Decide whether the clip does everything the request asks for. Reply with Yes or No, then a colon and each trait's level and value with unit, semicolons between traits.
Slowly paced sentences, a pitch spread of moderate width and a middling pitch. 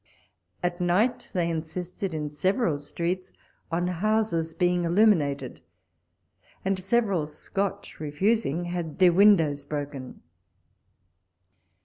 Yes: slow, 95 wpm; average, 4.0 semitones; medium, 175 Hz